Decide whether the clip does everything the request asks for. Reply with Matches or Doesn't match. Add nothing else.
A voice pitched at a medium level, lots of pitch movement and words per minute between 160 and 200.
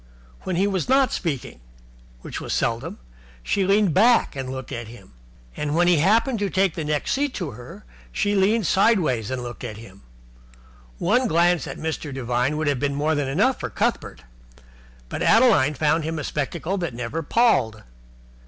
Matches